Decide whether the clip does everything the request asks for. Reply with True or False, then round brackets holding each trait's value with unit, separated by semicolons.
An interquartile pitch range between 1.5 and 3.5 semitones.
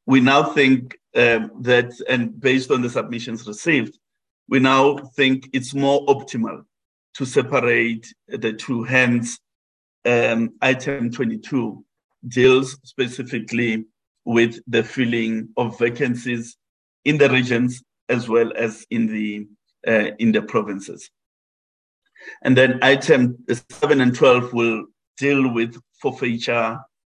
True (2.4 semitones)